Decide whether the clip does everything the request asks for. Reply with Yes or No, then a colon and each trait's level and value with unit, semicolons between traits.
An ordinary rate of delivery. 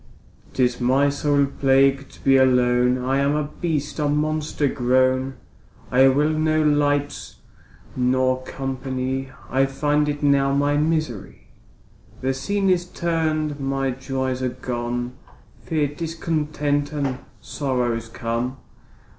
No: slow, 120 wpm